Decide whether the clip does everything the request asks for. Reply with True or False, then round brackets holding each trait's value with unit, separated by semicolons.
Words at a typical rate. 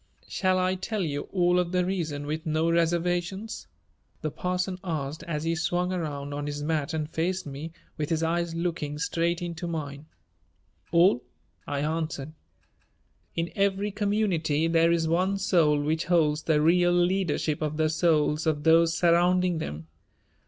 True (155 wpm)